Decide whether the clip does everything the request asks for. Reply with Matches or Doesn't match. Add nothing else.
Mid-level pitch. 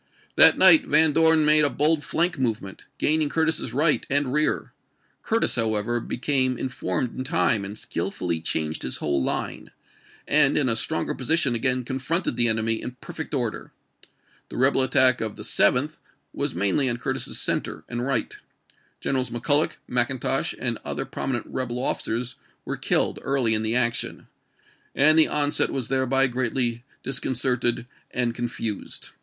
Doesn't match